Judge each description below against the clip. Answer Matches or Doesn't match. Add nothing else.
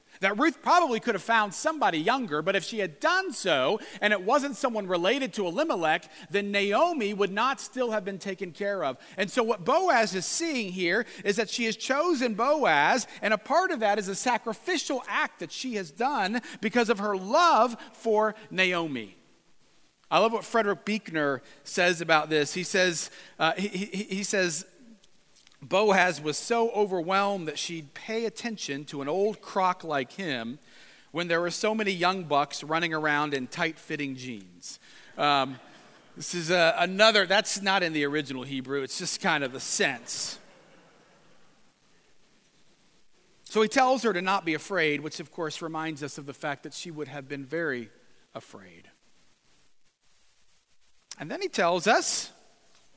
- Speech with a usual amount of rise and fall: Doesn't match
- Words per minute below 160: Doesn't match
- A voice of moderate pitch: Doesn't match